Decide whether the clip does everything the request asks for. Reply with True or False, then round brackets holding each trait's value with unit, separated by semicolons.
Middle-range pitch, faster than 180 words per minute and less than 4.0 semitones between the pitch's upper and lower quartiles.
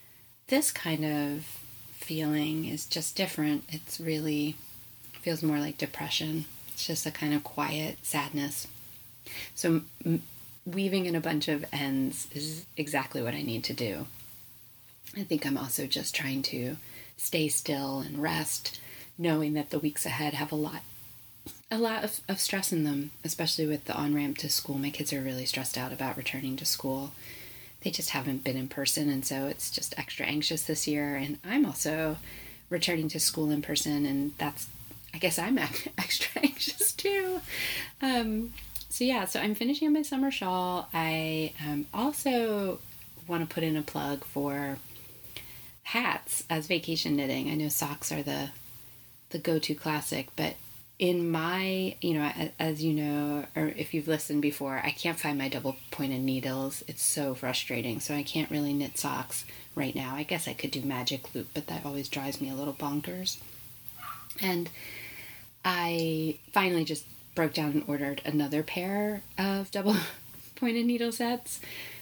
False (150 Hz; 170 wpm; 3.6 semitones)